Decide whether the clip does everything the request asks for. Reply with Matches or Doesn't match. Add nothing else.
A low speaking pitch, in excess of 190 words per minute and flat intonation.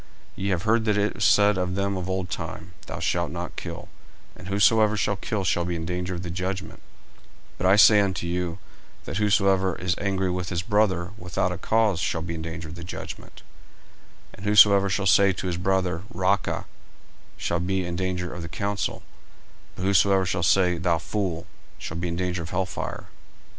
Matches